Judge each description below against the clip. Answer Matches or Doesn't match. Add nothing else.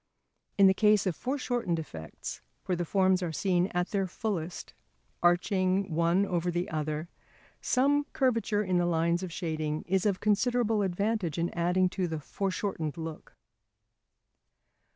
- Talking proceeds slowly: Doesn't match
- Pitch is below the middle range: Doesn't match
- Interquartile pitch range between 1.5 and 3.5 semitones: Matches